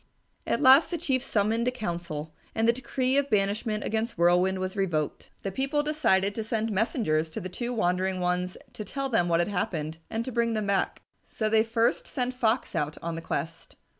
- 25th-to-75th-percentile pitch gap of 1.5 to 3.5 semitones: No, average, 5.0 semitones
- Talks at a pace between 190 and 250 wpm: Yes, average, 200 wpm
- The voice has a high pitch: Yes, high, 215 Hz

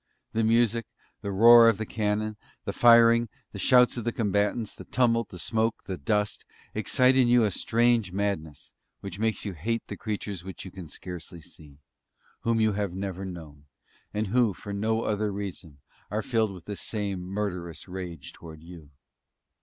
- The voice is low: Yes, low, 105 Hz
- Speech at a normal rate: Yes, average, 175 wpm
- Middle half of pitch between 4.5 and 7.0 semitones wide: No, average, 3.9 semitones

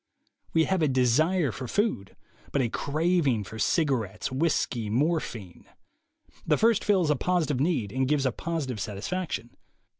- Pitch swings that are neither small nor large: No, wide, 6.1 semitones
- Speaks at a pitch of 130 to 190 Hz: Yes, medium, 140 Hz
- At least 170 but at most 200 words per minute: No, average, 145 wpm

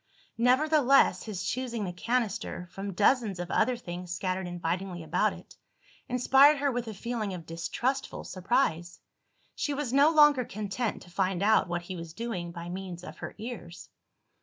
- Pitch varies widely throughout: Yes, wide, 6.0 semitones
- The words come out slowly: No, average, 160 wpm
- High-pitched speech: Yes, high, 200 Hz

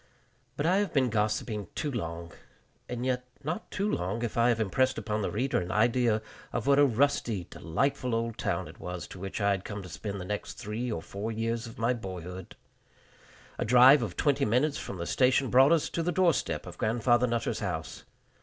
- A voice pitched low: Yes, low, 115 Hz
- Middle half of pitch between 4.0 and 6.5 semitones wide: Yes, average, 4.4 semitones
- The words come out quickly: Yes, fast, 210 wpm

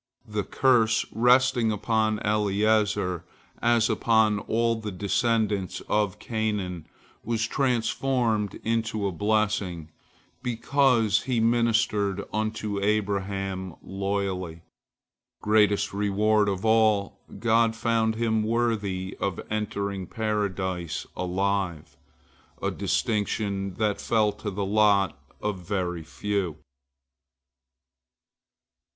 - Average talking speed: No, slow, 95 wpm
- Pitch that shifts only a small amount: Yes, narrow, 2.3 semitones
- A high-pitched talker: No, low, 105 Hz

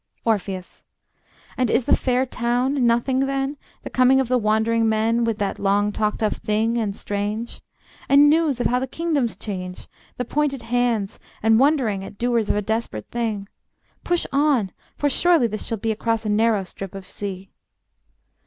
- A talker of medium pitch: No, high, 230 Hz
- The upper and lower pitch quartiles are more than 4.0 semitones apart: No, average, 3.6 semitones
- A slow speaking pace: No, average, 170 wpm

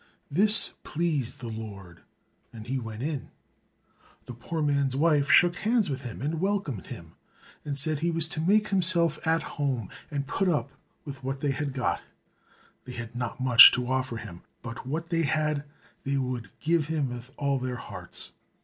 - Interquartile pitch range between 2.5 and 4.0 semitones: No, average, 4.5 semitones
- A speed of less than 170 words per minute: No, average, 175 wpm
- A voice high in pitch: No, medium, 140 Hz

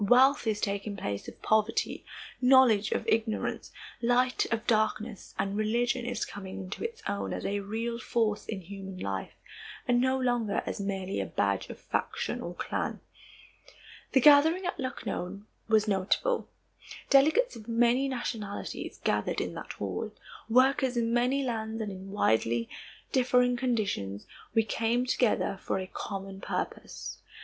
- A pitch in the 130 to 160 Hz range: No, high, 225 Hz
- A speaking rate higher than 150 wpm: No, average, 145 wpm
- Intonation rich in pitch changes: No, average, 3.9 semitones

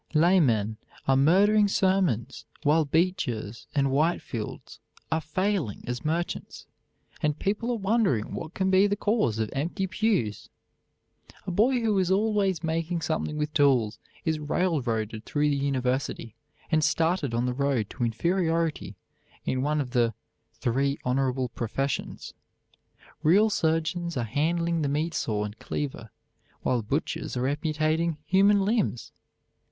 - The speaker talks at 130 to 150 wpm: Yes, slow, 135 wpm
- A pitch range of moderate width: No, wide, 6.3 semitones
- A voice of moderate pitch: Yes, medium, 155 Hz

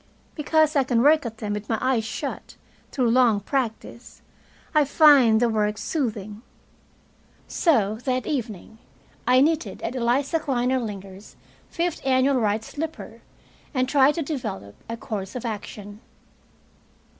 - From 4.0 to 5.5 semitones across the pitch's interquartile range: Yes, average, 4.5 semitones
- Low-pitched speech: No, high, 245 Hz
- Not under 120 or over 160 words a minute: Yes, slow, 135 wpm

